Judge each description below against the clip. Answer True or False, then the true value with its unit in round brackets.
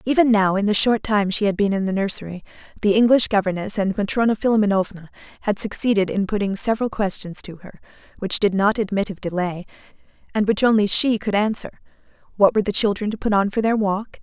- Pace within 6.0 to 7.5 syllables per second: True (6.2 syllables/s)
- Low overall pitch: False (205 Hz)